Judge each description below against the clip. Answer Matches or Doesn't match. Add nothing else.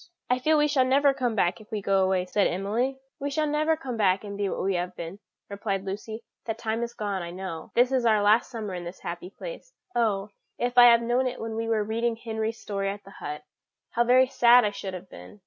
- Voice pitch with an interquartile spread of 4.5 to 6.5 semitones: Doesn't match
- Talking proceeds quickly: Matches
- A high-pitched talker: Matches